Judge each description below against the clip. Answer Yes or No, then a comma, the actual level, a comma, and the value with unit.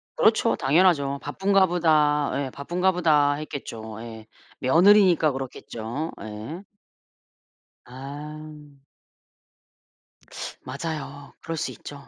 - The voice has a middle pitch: Yes, medium, 145 Hz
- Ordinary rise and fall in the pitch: Yes, average, 4.0 semitones